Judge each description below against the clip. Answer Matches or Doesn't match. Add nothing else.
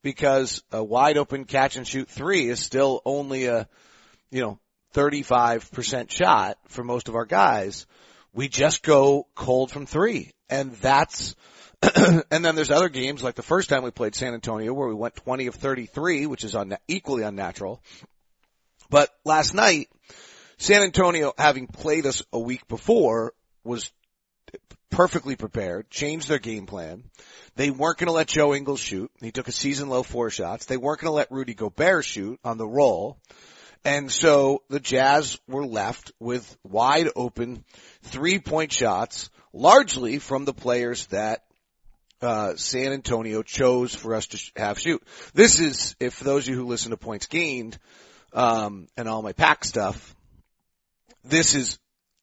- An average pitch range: Matches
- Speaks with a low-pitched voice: Matches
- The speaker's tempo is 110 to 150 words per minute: Doesn't match